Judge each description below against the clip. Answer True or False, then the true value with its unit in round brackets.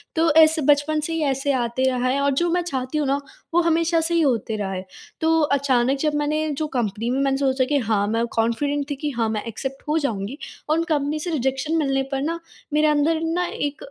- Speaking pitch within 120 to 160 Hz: False (285 Hz)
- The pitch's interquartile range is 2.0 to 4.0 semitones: True (3.6 semitones)